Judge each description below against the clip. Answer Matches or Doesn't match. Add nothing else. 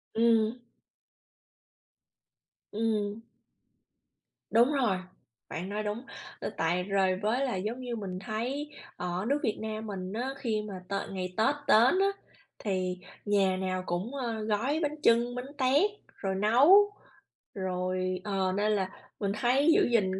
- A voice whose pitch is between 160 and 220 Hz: Matches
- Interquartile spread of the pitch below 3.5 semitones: Doesn't match